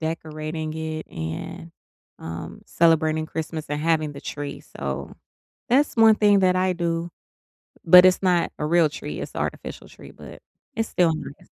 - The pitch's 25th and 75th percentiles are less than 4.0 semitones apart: Yes, average, 2.7 semitones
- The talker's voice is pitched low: No, medium, 160 Hz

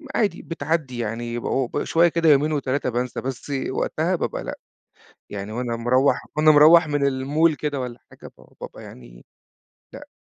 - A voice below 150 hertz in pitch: Yes, low, 135 Hz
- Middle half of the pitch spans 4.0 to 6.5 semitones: Yes, average, 4.4 semitones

